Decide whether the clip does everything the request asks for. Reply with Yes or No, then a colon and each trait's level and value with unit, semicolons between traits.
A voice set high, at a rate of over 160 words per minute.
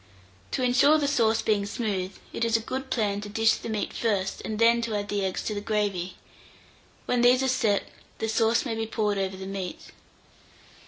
Yes: high, 220 Hz; fast, 205 wpm